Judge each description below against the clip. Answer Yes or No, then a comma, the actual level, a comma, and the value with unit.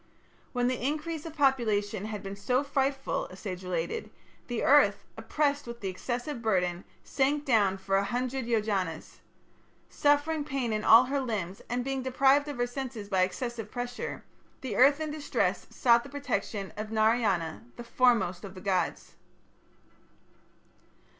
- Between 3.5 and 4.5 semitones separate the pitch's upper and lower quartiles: No, average, 5.2 semitones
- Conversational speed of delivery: Yes, average, 155 wpm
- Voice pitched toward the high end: Yes, high, 240 Hz